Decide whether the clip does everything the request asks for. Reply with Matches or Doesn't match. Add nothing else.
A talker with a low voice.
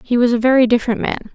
Doesn't match